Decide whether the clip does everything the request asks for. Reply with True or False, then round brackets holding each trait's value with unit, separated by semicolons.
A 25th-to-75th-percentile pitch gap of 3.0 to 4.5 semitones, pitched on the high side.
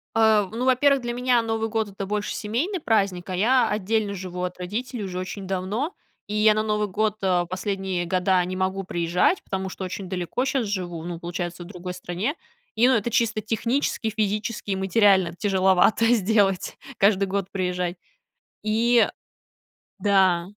True (3.3 semitones; 200 Hz)